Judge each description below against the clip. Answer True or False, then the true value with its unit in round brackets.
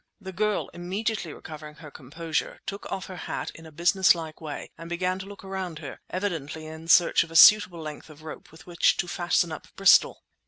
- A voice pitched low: False (170 Hz)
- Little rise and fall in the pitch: False (3.1 semitones)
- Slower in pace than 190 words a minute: False (200 wpm)